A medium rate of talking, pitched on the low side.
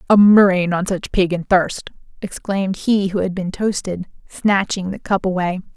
No: average, 165 wpm; high, 190 Hz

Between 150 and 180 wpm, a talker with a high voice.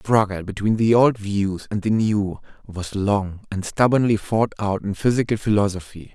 No: average, 175 wpm; low, 105 Hz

